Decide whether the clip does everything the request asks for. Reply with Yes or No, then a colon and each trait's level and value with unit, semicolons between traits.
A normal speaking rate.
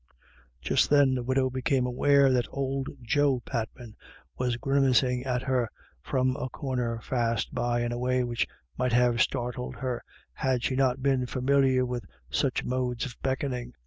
Yes: average, 165 wpm